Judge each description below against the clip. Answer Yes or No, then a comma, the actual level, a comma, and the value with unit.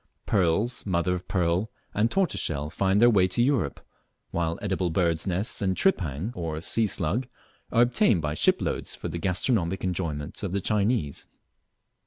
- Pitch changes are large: No, average, 4.3 semitones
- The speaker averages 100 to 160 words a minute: Yes, average, 155 wpm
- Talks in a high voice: No, very low, 95 Hz